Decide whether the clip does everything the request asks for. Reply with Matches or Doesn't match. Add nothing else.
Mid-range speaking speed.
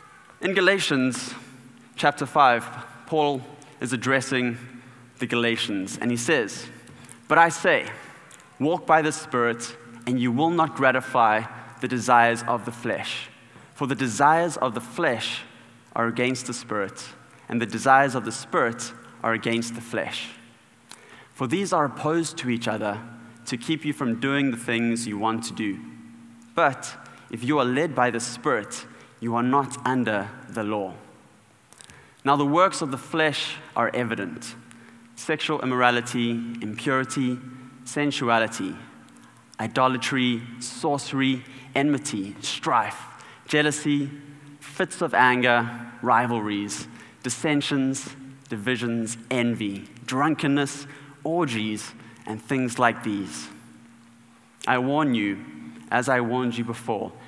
Doesn't match